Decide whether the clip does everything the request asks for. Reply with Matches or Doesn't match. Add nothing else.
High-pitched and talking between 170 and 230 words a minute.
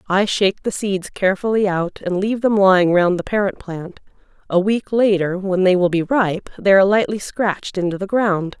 Matches